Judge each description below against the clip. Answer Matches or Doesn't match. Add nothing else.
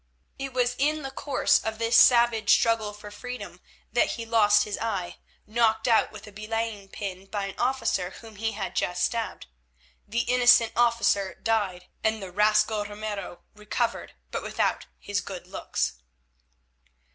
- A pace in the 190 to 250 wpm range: Doesn't match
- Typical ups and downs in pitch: Doesn't match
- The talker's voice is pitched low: Doesn't match